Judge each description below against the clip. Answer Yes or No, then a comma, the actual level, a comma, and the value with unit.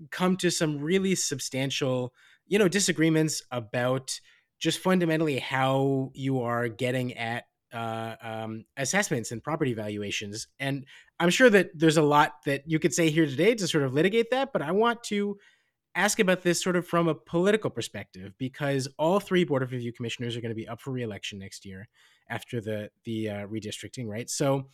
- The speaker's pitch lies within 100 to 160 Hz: Yes, low, 135 Hz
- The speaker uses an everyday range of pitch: No, wide, 6.4 semitones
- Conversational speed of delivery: Yes, average, 185 wpm